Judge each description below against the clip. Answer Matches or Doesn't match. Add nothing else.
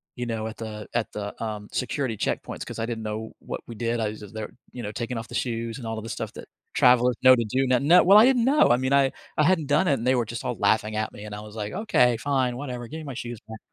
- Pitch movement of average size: Matches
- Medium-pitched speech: Doesn't match